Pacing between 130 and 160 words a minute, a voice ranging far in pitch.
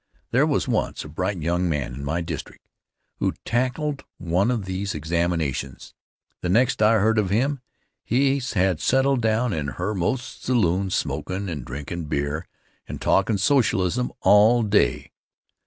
Yes: average, 150 wpm; wide, 6.4 semitones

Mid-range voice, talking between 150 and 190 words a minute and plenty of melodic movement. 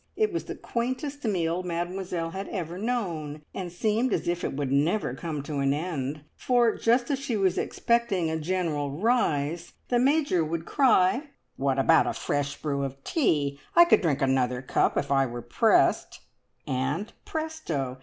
Yes: medium, 170 Hz; average, 170 wpm; wide, 8.4 semitones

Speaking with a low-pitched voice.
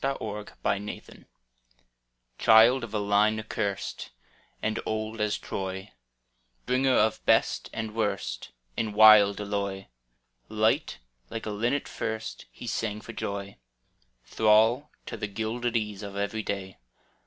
Yes: low, 105 Hz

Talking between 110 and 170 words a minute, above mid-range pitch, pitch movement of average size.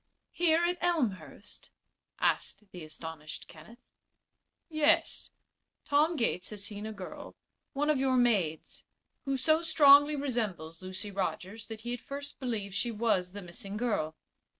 No: average, 140 wpm; high, 225 Hz; wide, 7.1 semitones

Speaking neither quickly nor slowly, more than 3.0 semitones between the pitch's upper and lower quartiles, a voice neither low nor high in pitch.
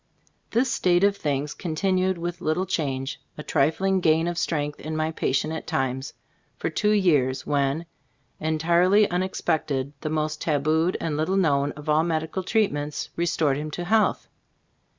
Yes: average, 160 wpm; average, 3.5 semitones; medium, 160 Hz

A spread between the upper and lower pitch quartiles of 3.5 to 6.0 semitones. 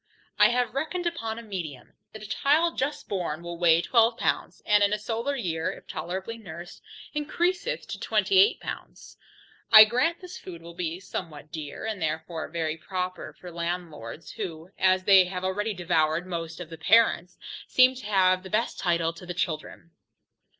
Yes: average, 5.3 semitones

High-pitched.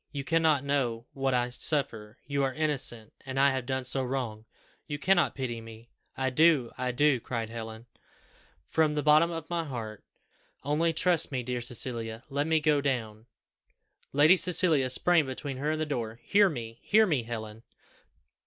No: low, 135 Hz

